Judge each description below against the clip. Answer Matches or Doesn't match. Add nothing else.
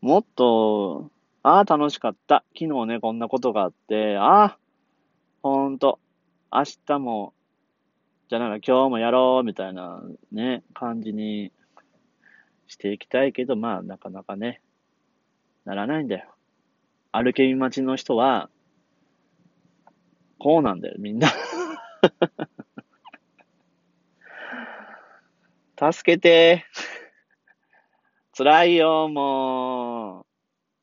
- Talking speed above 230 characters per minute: Doesn't match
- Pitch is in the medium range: Doesn't match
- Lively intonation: Doesn't match